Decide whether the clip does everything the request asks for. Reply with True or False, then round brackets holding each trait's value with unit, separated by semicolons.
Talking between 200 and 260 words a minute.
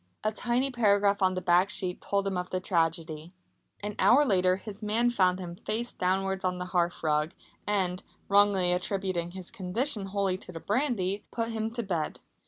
False (180 wpm)